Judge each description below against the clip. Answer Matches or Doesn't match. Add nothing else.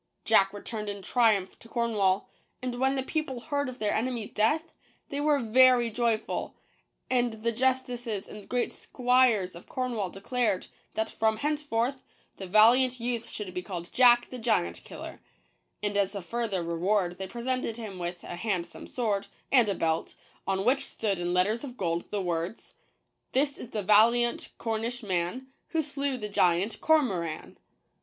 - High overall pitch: Matches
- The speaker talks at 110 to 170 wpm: Matches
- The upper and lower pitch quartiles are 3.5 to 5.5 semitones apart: Matches